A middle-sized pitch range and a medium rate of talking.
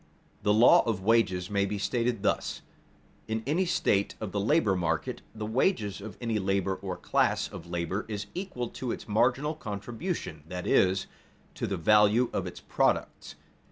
Yes: average, 3.7 semitones; average, 165 wpm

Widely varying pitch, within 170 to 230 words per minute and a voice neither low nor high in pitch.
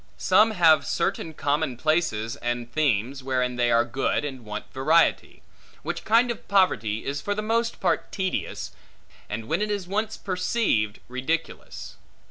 No: wide, 8.1 semitones; average, 150 wpm; medium, 145 Hz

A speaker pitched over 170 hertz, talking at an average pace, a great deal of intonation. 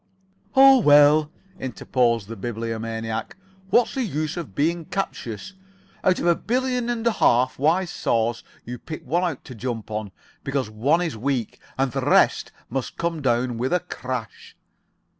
No: low, 135 Hz; average, 160 wpm; wide, 7.0 semitones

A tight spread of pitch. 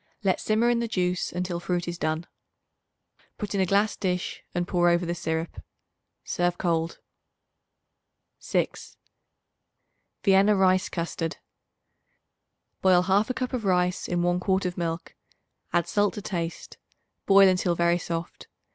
Yes: narrow, 2.2 semitones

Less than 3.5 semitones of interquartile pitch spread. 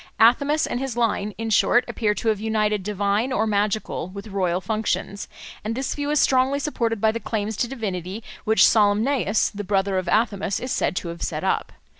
Yes: average, 2.7 semitones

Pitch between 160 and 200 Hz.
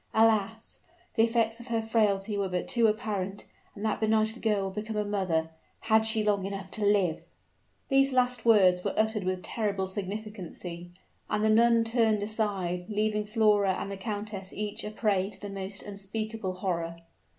No: high, 210 Hz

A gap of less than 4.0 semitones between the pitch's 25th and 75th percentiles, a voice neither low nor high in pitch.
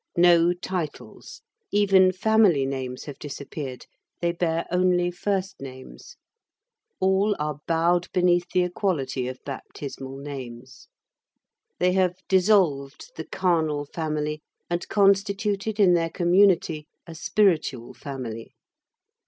No: average, 4.9 semitones; medium, 170 Hz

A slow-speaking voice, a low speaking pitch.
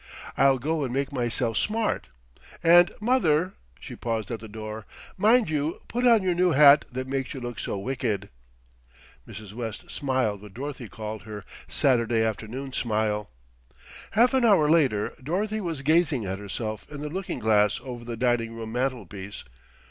No: average, 165 wpm; low, 130 Hz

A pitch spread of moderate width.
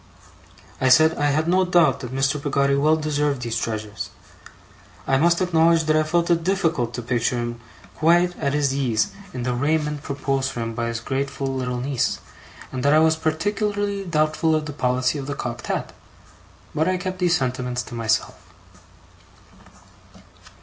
Yes: average, 4.2 semitones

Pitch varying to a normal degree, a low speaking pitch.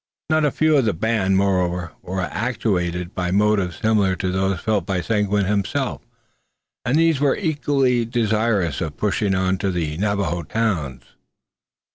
Yes: average, 4.0 semitones; low, 100 Hz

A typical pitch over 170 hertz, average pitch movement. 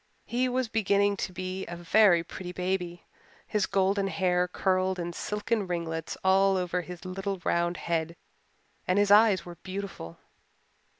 No: medium, 185 Hz; narrow, 2.3 semitones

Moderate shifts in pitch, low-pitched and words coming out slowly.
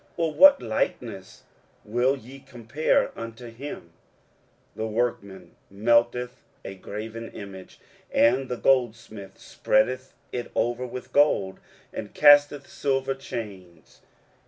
Yes: average, 3.9 semitones; low, 120 Hz; slow, 110 wpm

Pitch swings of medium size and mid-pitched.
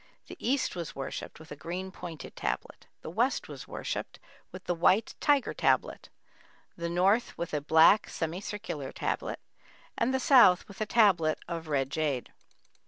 Yes: average, 5.0 semitones; medium, 175 Hz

